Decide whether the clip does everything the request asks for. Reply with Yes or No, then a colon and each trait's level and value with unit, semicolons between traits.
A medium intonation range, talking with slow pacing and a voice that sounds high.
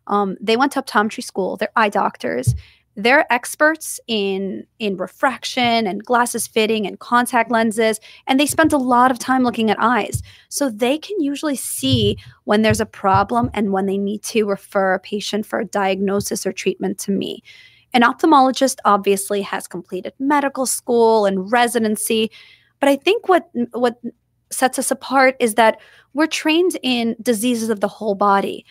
No: average, 4.3 semitones; average, 170 wpm; high, 230 Hz